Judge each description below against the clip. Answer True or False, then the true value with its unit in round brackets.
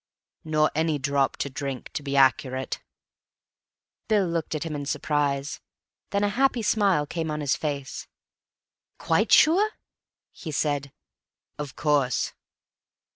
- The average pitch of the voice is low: False (150 Hz)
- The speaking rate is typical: False (130 wpm)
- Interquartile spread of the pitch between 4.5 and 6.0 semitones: False (3.1 semitones)